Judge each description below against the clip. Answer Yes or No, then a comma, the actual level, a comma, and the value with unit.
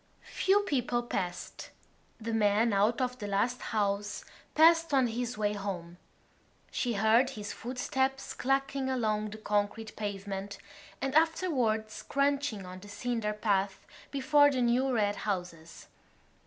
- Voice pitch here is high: Yes, high, 225 Hz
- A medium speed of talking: No, slow, 130 wpm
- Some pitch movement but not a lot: Yes, average, 4.4 semitones